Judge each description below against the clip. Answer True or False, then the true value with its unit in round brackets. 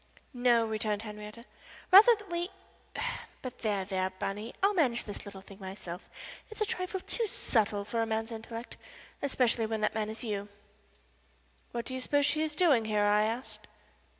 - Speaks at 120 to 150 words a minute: False (175 wpm)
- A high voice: True (225 Hz)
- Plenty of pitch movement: False (5.0 semitones)